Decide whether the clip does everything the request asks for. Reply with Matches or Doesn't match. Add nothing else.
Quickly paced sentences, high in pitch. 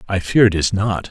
Doesn't match